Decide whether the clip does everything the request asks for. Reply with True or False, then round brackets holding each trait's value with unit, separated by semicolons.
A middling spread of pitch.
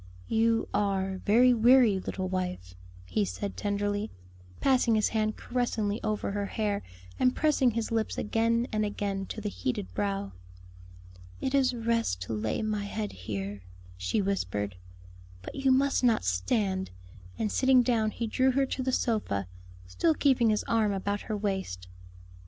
True (3.7 semitones)